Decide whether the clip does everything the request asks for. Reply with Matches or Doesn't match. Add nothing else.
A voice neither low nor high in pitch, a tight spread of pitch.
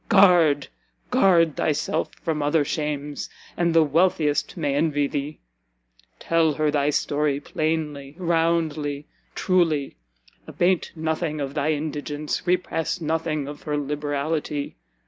Matches